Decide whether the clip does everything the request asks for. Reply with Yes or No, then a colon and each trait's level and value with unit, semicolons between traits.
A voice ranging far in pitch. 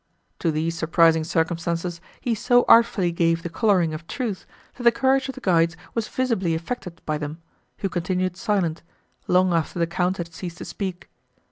No: average, 3.4 semitones